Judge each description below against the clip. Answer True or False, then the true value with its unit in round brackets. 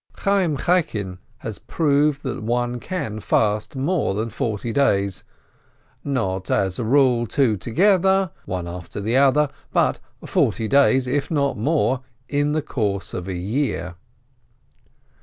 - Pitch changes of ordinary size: False (5.8 semitones)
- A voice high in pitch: False (125 Hz)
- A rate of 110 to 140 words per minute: True (135 wpm)